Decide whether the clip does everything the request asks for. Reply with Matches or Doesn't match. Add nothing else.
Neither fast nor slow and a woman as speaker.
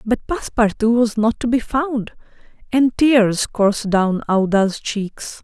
Matches